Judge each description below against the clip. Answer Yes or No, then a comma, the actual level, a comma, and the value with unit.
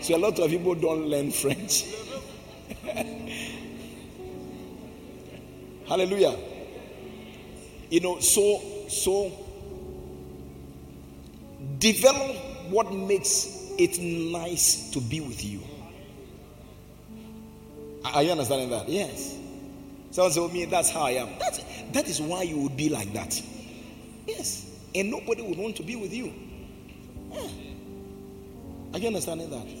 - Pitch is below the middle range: No, medium, 165 Hz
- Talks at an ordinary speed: No, slow, 115 wpm